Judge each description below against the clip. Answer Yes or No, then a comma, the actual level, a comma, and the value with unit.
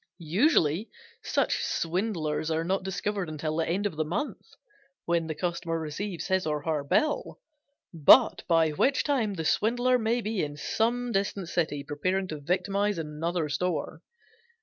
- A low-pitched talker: No, medium, 175 Hz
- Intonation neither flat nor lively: Yes, average, 4.7 semitones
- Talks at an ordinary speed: Yes, average, 150 wpm